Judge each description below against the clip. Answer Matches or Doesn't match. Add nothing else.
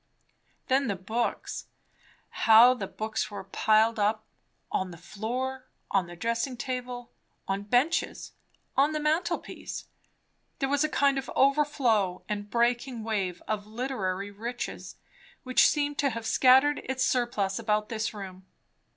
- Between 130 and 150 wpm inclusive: Matches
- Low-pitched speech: Doesn't match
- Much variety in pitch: Doesn't match